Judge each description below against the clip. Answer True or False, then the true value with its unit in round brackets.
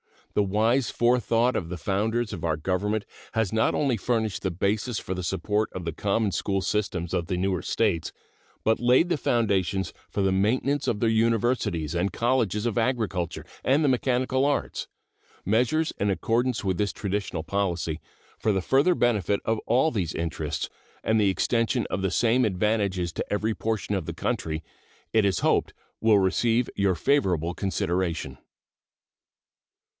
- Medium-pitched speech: False (105 Hz)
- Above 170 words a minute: False (160 wpm)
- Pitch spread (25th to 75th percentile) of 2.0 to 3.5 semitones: False (4.0 semitones)